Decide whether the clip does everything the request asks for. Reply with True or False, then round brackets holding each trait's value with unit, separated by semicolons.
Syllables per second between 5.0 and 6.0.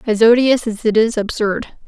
False (4.7 syllables/s)